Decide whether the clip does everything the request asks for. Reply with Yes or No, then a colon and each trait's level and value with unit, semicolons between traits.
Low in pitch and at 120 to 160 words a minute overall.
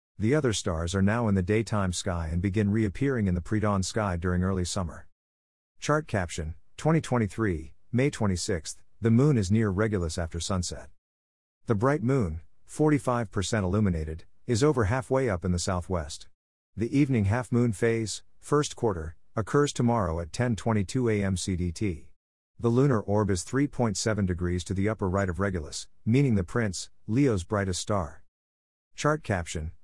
Yes: low, 100 Hz; average, 155 wpm